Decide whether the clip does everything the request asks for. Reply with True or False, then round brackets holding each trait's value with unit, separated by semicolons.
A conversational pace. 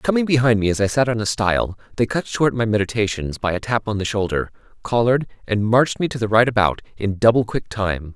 False (235 wpm)